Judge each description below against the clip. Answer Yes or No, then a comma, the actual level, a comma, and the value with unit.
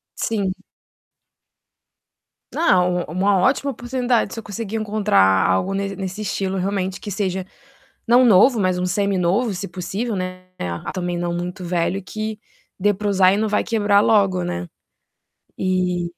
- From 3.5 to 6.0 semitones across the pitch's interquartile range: No, average, 2.7 semitones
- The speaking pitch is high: Yes, high, 195 Hz